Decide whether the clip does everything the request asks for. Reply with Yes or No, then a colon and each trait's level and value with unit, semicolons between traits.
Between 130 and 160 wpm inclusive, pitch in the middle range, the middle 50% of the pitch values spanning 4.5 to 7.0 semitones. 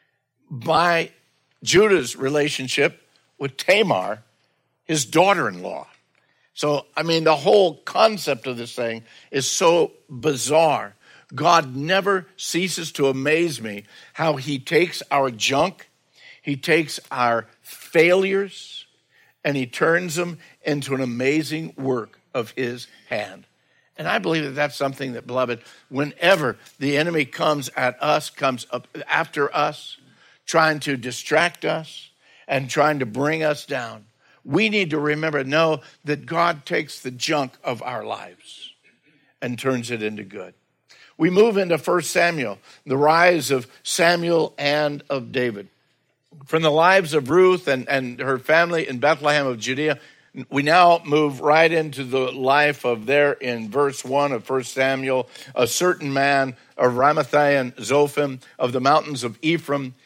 No: average, 145 wpm; medium, 145 Hz; average, 3.3 semitones